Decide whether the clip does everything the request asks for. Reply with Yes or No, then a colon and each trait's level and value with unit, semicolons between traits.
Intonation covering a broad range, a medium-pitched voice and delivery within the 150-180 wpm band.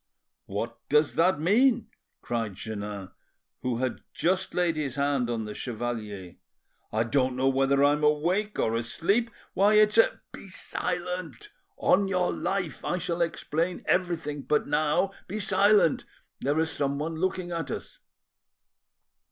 No: wide, 6.3 semitones; medium, 155 Hz; average, 140 wpm